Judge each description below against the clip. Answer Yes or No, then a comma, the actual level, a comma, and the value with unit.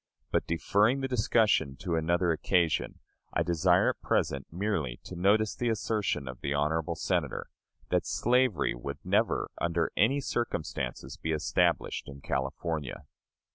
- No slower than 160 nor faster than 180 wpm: No, slow, 135 wpm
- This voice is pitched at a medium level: No, very low, 85 Hz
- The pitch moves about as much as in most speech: No, wide, 6.2 semitones